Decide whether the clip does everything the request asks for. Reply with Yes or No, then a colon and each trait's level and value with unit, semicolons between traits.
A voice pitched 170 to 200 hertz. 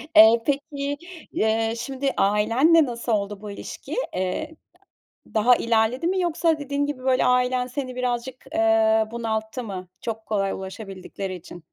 No: high, 230 Hz